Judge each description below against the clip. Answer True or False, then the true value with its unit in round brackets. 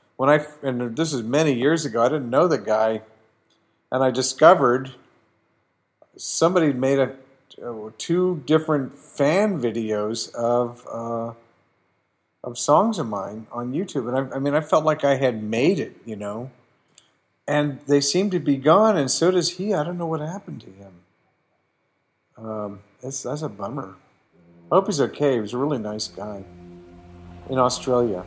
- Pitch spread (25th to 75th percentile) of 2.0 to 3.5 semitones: False (5.1 semitones)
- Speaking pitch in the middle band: False (130 Hz)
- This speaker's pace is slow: False (165 wpm)